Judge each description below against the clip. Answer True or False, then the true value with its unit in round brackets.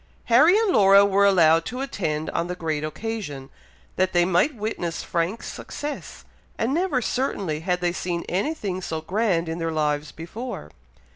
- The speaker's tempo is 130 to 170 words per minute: True (165 wpm)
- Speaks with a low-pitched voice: False (180 Hz)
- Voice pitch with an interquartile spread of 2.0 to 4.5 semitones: False (5.6 semitones)